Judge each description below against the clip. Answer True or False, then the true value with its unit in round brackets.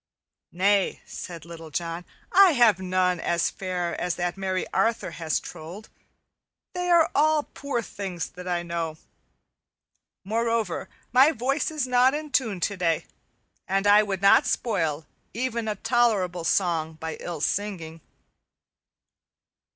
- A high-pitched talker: True (195 Hz)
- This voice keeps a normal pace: False (130 wpm)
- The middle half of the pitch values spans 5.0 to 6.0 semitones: True (5.4 semitones)